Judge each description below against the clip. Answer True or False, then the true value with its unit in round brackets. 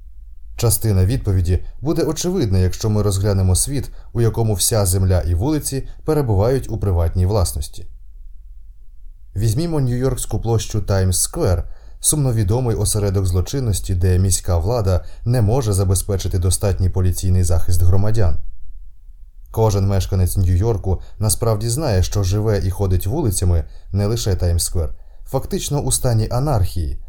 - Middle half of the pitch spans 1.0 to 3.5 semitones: False (4.0 semitones)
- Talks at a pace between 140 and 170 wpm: False (120 wpm)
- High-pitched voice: False (100 Hz)